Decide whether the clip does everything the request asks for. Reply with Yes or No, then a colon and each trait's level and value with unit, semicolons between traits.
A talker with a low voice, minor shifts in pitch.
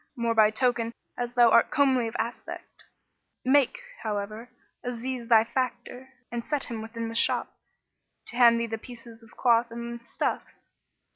No: high, 235 Hz; narrow, 1.4 semitones